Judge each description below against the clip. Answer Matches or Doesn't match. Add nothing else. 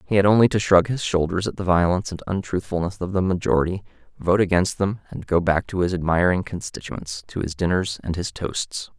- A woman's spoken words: Doesn't match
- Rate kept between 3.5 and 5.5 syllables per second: Doesn't match